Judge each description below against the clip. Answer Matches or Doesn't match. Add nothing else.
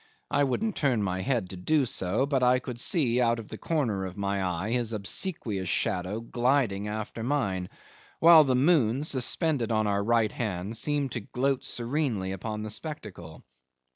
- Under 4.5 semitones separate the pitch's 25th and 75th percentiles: Doesn't match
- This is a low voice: Matches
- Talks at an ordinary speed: Matches